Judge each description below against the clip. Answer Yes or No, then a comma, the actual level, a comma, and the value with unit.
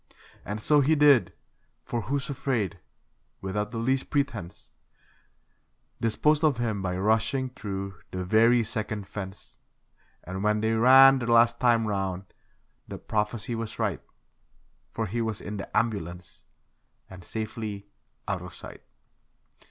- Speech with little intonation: No, average, 3.3 semitones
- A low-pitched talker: Yes, low, 110 Hz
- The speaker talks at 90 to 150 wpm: Yes, slow, 135 wpm